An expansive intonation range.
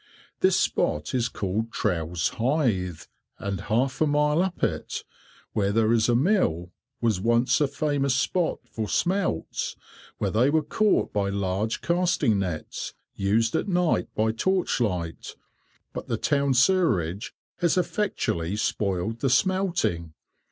Yes: wide, 7.7 semitones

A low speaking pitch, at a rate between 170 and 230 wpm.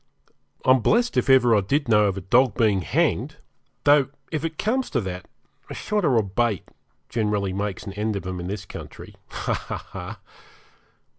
Yes: low, 110 Hz; average, 180 wpm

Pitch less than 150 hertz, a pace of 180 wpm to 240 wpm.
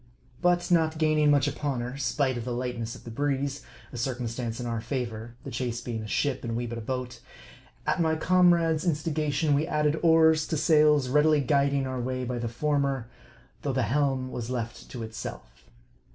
Yes: low, 135 Hz; average, 190 wpm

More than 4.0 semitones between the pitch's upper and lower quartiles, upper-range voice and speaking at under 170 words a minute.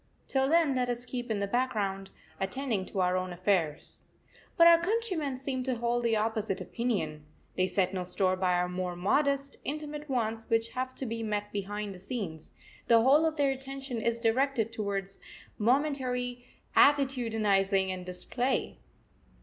Yes: wide, 5.4 semitones; high, 230 Hz; average, 160 wpm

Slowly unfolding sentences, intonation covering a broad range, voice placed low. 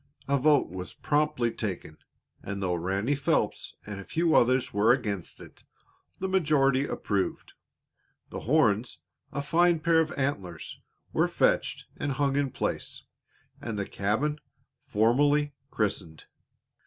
Yes: slow, 130 wpm; wide, 6.5 semitones; low, 130 Hz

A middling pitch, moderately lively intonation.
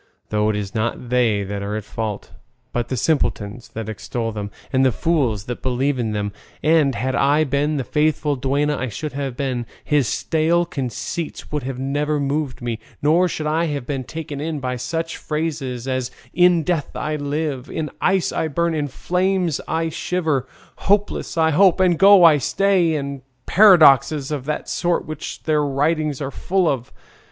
Yes: medium, 145 Hz; average, 4.2 semitones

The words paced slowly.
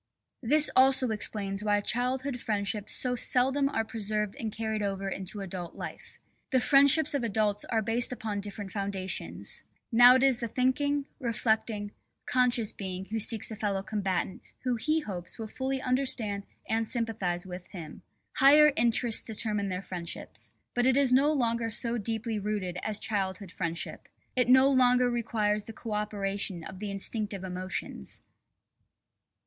No: average, 155 wpm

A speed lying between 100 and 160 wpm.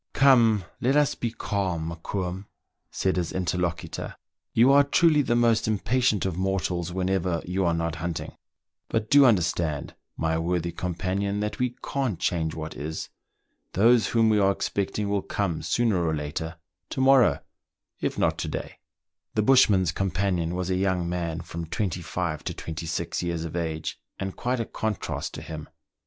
No: average, 170 wpm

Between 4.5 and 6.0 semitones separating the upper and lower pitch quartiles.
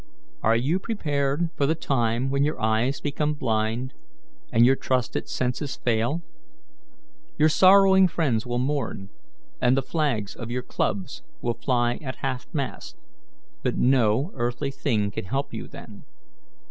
No: average, 3.9 semitones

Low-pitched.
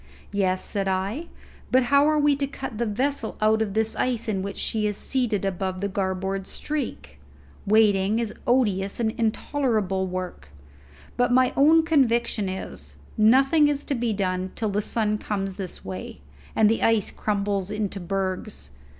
No: high, 210 Hz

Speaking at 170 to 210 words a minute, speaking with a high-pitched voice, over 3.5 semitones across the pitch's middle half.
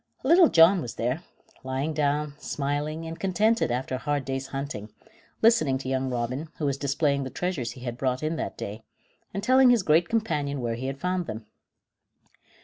No: average, 185 wpm; medium, 145 Hz; average, 4.5 semitones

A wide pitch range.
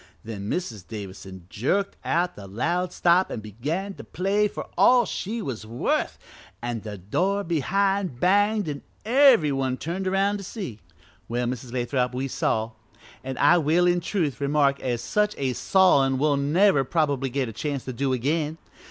Yes: wide, 7.2 semitones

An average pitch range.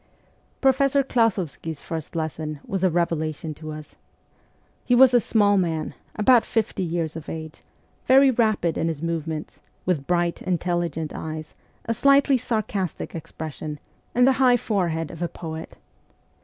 No: wide, 6.2 semitones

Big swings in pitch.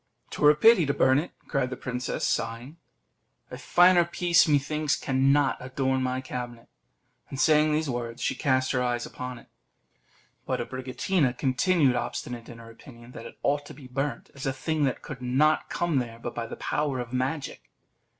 No: average, 3.3 semitones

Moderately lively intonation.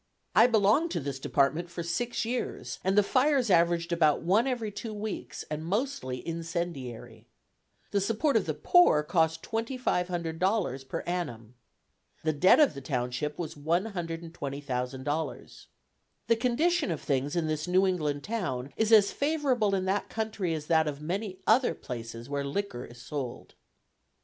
No: wide, 6.8 semitones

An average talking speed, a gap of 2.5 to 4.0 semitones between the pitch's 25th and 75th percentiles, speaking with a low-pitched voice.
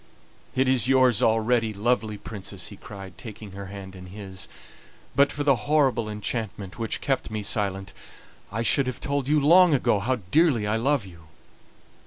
No: average, 170 wpm; average, 4.8 semitones; low, 110 Hz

